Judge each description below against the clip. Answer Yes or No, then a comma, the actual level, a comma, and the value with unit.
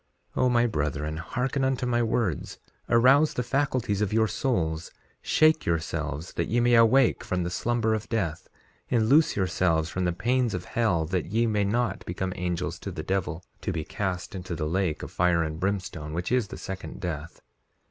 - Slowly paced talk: No, average, 190 wpm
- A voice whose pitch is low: Yes, very low, 95 Hz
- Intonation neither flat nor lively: No, wide, 5.9 semitones